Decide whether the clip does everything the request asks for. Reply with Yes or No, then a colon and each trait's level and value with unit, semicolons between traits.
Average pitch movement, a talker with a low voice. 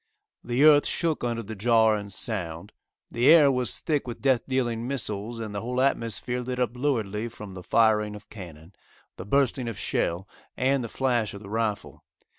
Yes: average, 3.4 semitones; low, 115 Hz